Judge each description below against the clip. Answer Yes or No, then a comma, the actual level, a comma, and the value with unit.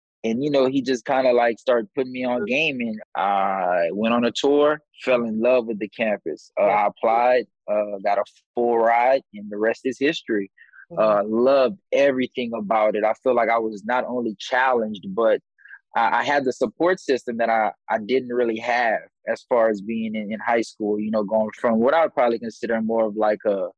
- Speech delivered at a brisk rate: Yes, fast, 215 wpm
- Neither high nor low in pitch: No, low, 115 Hz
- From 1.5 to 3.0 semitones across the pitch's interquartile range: Yes, average, 2.7 semitones